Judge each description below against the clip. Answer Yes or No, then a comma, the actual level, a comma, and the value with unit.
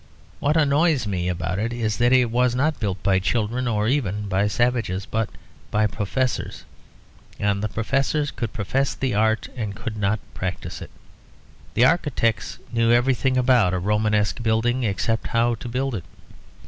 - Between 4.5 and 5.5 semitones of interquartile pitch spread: No, average, 3.5 semitones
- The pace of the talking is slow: No, average, 160 wpm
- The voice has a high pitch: No, low, 115 Hz